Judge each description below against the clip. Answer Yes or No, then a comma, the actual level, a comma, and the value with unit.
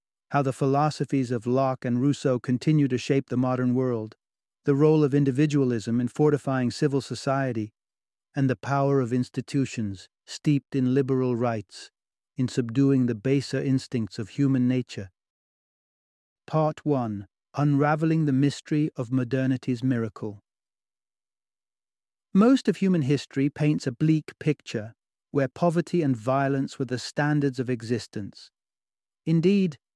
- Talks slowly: Yes, slow, 130 wpm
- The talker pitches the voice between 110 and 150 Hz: Yes, low, 135 Hz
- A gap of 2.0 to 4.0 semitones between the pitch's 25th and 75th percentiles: Yes, average, 2.8 semitones